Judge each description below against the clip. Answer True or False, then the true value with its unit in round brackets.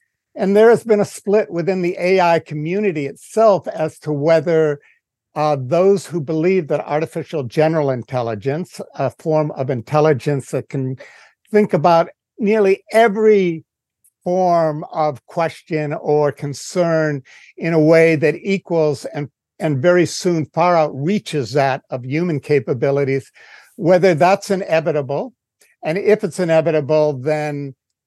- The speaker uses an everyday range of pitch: True (3.8 semitones)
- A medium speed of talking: False (130 wpm)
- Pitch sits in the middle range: True (160 Hz)